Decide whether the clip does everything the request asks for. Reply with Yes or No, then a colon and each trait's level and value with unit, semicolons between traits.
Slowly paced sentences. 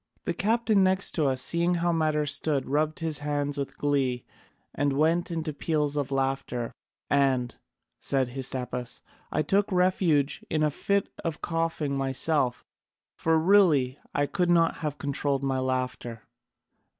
No: average, 145 wpm